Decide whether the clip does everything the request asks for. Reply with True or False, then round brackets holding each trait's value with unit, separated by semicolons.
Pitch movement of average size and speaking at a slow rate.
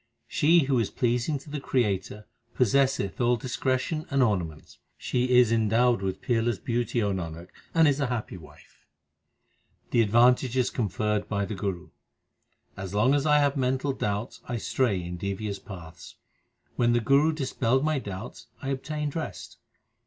False (4.7 semitones; 155 wpm)